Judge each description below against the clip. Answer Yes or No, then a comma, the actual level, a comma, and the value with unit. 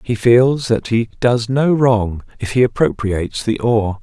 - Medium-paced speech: Yes, average, 180 wpm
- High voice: No, low, 115 Hz